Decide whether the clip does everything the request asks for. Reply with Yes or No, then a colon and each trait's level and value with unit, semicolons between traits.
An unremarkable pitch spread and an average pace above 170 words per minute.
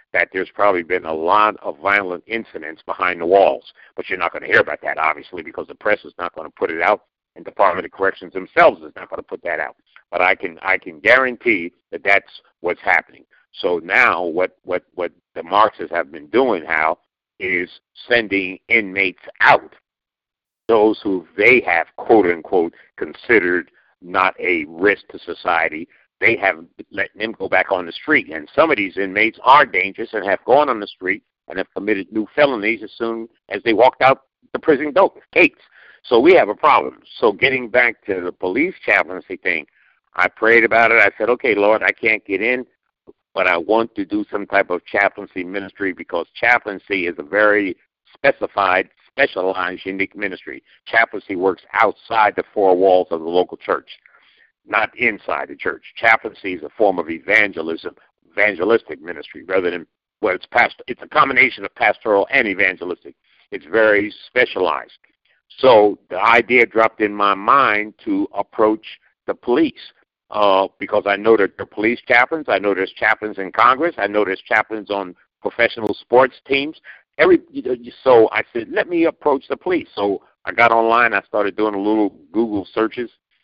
Yes: average, 3.4 semitones; average, 180 wpm